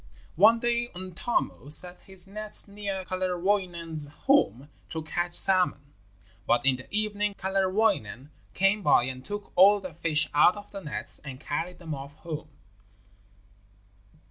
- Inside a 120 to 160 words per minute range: Yes, average, 140 wpm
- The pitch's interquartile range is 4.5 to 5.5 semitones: Yes, average, 5.1 semitones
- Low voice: No, medium, 180 Hz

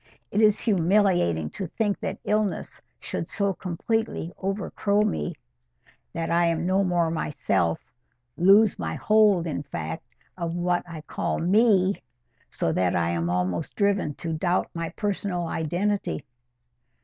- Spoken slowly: Yes, slow, 130 wpm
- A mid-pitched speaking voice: Yes, medium, 175 Hz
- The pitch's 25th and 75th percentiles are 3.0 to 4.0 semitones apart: No, wide, 5.5 semitones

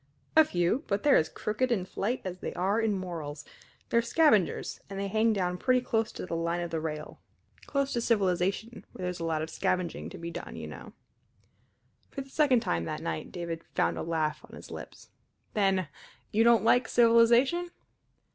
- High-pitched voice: Yes, high, 195 Hz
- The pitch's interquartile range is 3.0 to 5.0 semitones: No, wide, 5.6 semitones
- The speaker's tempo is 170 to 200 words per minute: Yes, average, 190 wpm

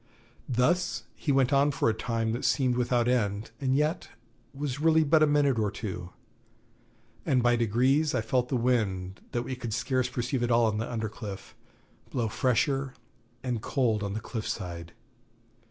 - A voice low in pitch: Yes, low, 120 Hz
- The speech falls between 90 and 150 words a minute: No, average, 175 wpm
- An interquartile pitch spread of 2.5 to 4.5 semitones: Yes, average, 3.4 semitones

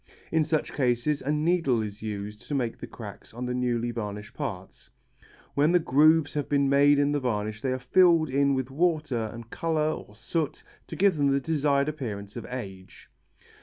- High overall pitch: No, low, 135 Hz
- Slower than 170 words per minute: No, average, 190 wpm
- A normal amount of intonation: Yes, average, 4.5 semitones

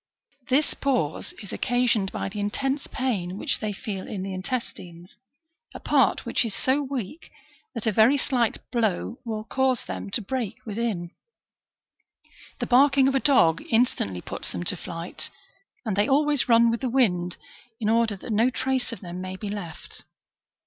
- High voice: Yes, high, 225 Hz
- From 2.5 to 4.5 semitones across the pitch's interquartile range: No, wide, 5.4 semitones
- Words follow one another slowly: No, average, 170 wpm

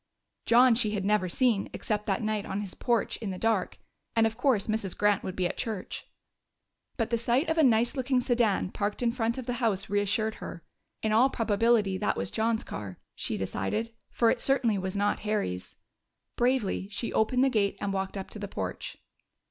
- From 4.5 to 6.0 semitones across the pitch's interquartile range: No, average, 3.0 semitones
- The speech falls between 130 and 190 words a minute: No, average, 200 wpm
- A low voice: No, high, 220 Hz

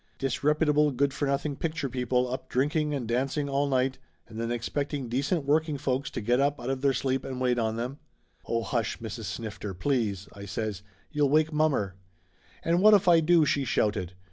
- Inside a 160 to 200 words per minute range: Yes, average, 195 wpm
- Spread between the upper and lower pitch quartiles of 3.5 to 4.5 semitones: Yes, average, 3.9 semitones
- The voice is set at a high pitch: No, low, 135 Hz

